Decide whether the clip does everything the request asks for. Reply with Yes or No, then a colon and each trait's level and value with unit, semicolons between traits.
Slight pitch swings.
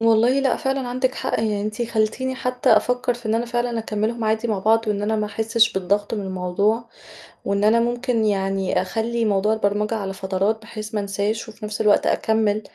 Yes: narrow, 2.2 semitones